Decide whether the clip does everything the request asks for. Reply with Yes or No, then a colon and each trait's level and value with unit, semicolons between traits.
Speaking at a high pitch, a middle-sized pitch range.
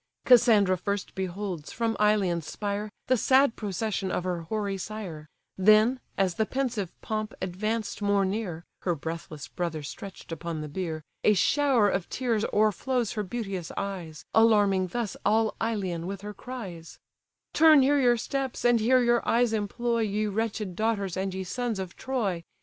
Yes: high, 205 Hz; average, 3.7 semitones